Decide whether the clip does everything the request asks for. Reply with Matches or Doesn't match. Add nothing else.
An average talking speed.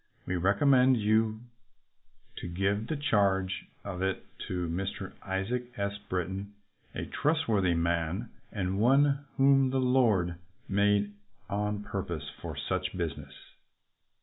Doesn't match